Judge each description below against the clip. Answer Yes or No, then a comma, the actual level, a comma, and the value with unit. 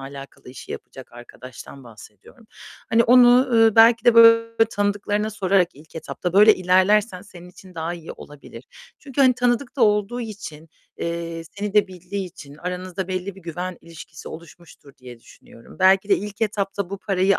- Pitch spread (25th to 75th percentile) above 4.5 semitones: No, average, 4.1 semitones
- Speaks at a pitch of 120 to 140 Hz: No, high, 190 Hz